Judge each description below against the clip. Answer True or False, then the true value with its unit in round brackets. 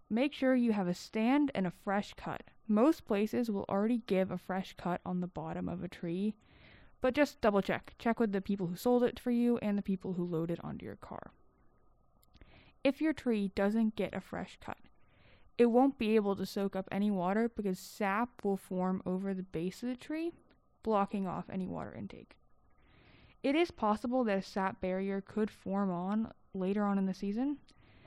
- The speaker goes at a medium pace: True (195 wpm)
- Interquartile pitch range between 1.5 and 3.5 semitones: False (3.9 semitones)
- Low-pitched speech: False (200 Hz)